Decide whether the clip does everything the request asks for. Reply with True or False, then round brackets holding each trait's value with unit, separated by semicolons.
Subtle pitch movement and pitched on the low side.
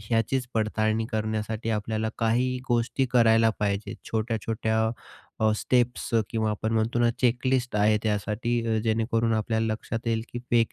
True (1.4 semitones; 115 Hz)